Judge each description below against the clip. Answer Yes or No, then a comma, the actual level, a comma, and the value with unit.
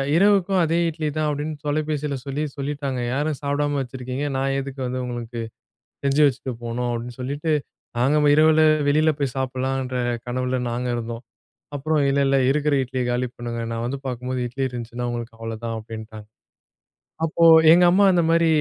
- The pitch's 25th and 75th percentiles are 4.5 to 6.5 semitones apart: No, average, 3.4 semitones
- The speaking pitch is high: No, low, 135 Hz